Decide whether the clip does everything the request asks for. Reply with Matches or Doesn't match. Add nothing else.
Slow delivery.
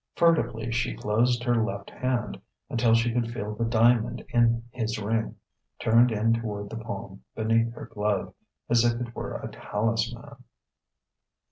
Doesn't match